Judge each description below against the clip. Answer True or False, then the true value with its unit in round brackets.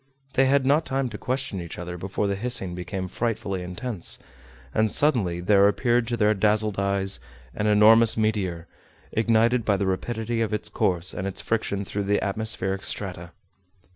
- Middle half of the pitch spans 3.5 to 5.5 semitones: False (3.1 semitones)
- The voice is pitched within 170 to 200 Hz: False (105 Hz)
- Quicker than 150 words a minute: True (170 wpm)